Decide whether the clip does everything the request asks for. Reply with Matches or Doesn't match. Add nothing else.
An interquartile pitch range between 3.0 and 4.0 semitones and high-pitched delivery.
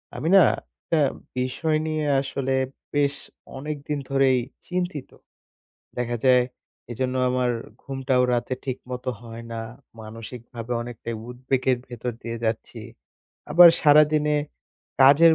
Doesn't match